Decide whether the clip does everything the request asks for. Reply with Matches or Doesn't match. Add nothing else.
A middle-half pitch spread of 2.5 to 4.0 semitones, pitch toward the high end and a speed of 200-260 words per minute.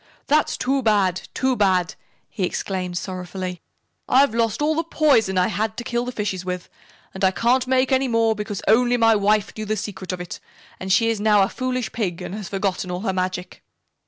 Doesn't match